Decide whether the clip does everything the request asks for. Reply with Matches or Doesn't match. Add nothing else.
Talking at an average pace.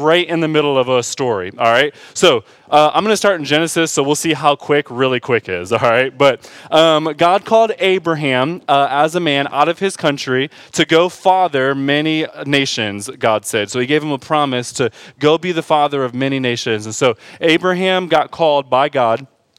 Doesn't match